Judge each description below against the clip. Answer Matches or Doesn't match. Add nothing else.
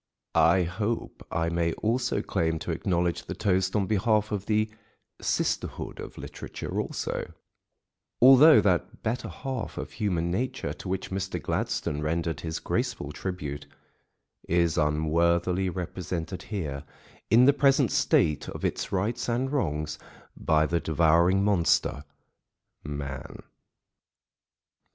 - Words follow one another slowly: Matches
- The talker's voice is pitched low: Matches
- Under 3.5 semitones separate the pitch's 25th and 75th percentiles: Doesn't match